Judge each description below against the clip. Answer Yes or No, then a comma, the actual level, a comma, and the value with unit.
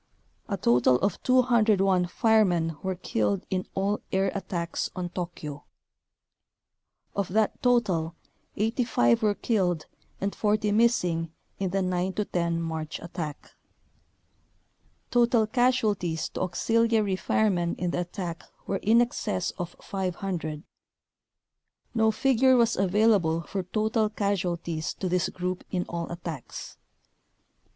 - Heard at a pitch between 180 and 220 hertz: Yes, high, 190 Hz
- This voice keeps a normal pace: No, slow, 120 wpm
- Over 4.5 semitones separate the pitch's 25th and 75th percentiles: No, average, 4.0 semitones